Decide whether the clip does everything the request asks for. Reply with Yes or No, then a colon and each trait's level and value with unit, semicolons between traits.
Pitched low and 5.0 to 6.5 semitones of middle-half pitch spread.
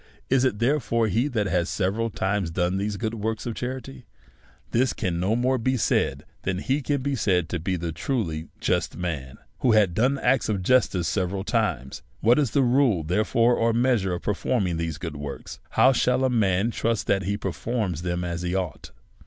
Yes: low, 105 Hz; wide, 5.5 semitones